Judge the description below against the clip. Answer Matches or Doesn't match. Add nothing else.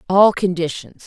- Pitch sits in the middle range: Matches